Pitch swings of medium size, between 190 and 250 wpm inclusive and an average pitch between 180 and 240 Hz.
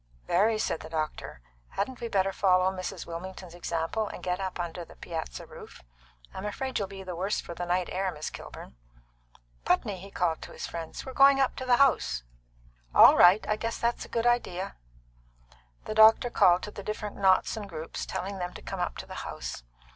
Yes: average, 3.6 semitones; average, 200 wpm; high, 190 Hz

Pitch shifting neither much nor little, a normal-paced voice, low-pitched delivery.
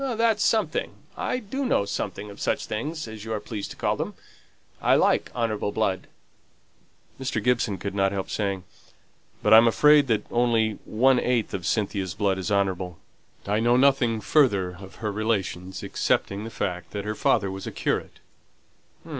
Yes: average, 3.7 semitones; average, 170 wpm; low, 110 Hz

